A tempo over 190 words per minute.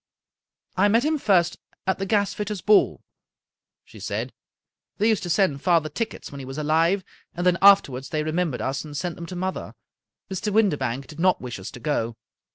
Yes: average, 200 wpm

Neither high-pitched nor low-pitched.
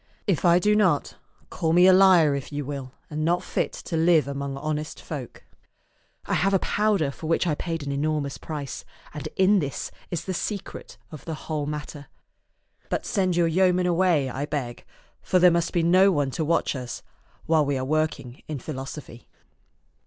Yes: medium, 155 Hz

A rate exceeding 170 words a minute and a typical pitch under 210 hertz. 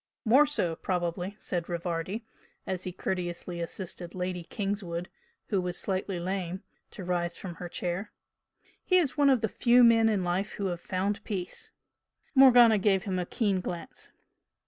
No: average, 160 wpm; medium, 185 Hz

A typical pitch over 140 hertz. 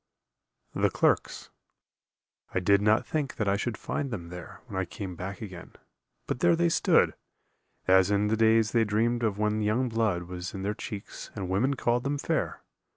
No: low, 105 Hz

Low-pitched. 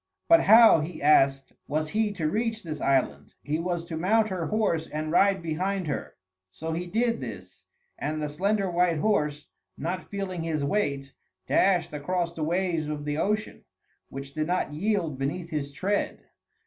No: medium, 170 Hz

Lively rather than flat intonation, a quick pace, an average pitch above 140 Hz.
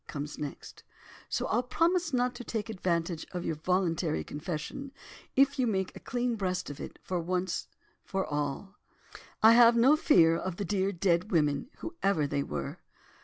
No: wide, 6.4 semitones; average, 165 wpm; medium, 185 Hz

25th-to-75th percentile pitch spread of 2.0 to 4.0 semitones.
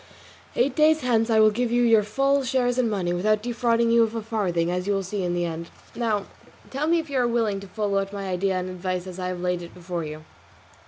No: average, 4.7 semitones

